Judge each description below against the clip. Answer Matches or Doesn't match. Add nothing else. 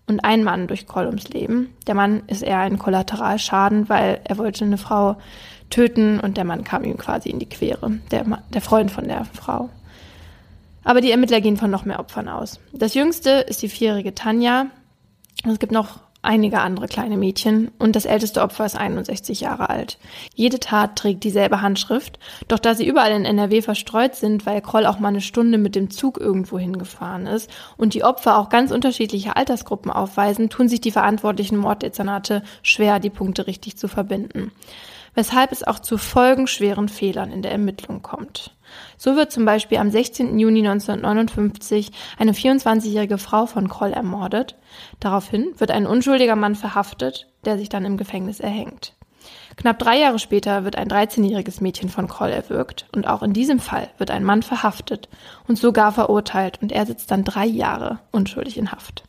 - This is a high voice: Matches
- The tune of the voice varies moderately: Doesn't match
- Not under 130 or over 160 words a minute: Doesn't match